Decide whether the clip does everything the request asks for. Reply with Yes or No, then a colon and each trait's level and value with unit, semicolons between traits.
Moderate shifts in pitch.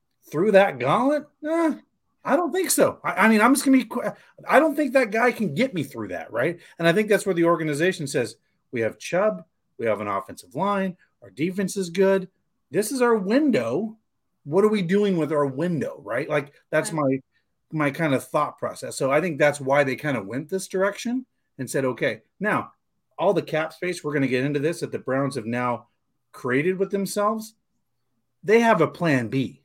No: wide, 6.7 semitones